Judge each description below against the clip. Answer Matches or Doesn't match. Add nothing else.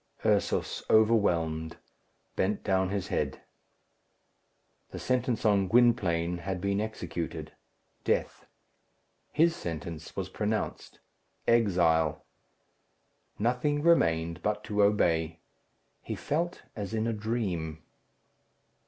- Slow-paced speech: Matches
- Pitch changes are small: Doesn't match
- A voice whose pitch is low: Matches